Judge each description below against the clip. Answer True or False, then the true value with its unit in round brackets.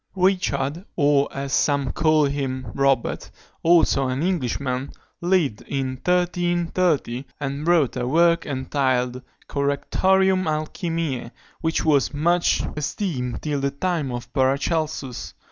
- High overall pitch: False (145 Hz)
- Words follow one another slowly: True (110 wpm)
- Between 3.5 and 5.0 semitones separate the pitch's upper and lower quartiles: True (4.2 semitones)